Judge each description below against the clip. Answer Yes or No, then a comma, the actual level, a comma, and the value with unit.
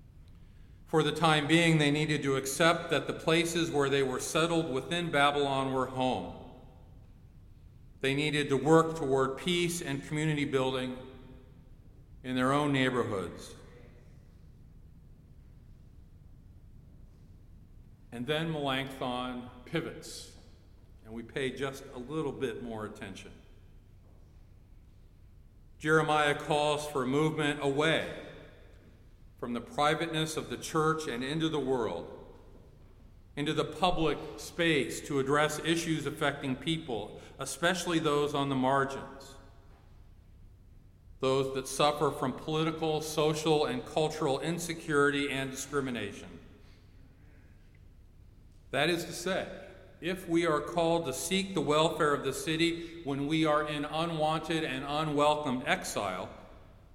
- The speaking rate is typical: No, slow, 115 wpm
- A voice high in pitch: No, low, 135 Hz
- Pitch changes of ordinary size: No, wide, 6.6 semitones